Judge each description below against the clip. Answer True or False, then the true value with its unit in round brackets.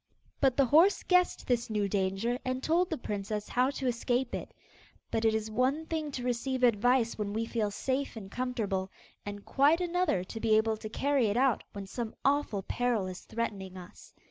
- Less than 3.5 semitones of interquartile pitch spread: False (4.2 semitones)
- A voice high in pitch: True (235 Hz)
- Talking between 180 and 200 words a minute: True (195 wpm)